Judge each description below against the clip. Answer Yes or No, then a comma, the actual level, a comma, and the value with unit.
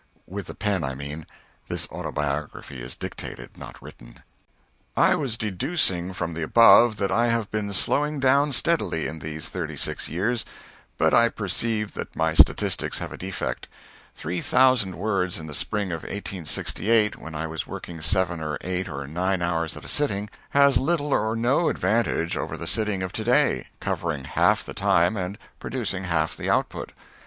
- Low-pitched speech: Yes, very low, 95 Hz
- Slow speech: No, average, 150 wpm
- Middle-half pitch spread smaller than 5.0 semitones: No, wide, 5.5 semitones